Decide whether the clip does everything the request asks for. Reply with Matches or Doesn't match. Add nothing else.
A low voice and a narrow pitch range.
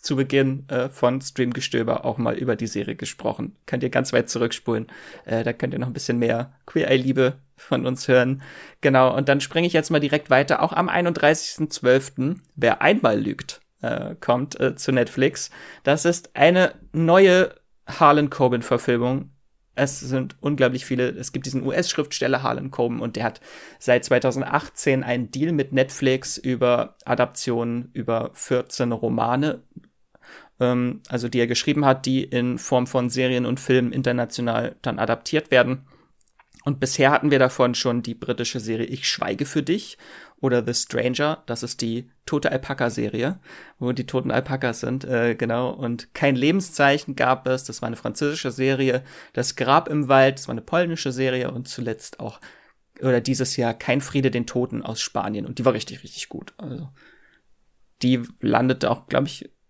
Matches